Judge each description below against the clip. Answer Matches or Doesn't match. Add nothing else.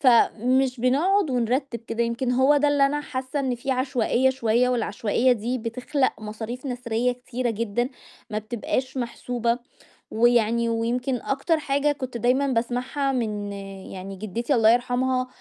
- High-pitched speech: Matches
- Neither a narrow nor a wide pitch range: Doesn't match